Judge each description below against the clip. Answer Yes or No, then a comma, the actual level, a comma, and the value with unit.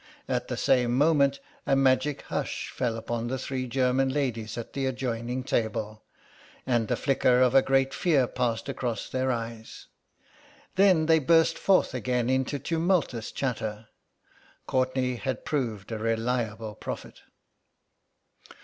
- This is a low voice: Yes, low, 130 Hz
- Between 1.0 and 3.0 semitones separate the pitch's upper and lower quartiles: Yes, average, 2.7 semitones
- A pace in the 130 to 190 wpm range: Yes, slow, 135 wpm